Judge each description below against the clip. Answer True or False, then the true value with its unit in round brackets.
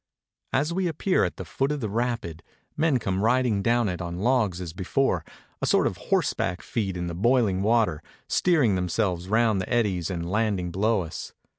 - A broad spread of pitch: False (5.0 semitones)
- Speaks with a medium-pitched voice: False (105 Hz)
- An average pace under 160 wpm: False (185 wpm)